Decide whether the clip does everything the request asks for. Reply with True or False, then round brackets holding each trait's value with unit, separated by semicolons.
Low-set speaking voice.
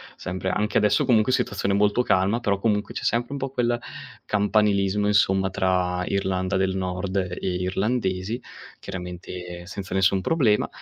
True (100 Hz)